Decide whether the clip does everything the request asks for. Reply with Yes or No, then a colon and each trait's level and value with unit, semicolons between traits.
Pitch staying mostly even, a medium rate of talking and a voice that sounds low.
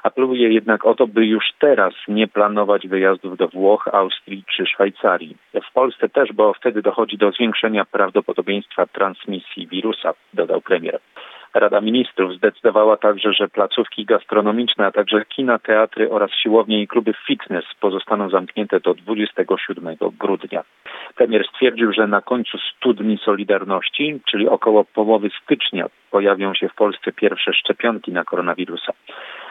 Yes: narrow, 2.3 semitones; average, 140 wpm; low, 105 Hz